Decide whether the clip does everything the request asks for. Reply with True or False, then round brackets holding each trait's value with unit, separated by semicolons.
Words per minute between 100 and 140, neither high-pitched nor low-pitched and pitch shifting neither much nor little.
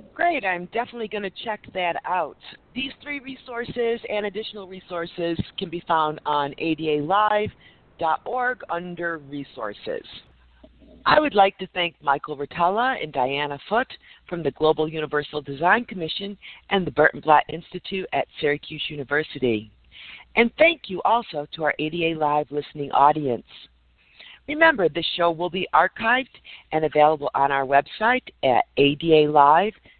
False (135 wpm; 170 Hz; 6.4 semitones)